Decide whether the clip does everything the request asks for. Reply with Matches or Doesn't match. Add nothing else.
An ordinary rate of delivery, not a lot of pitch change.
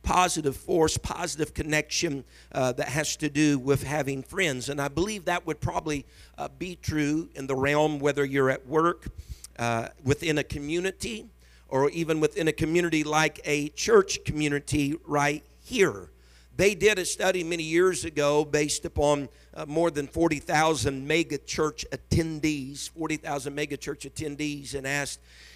Matches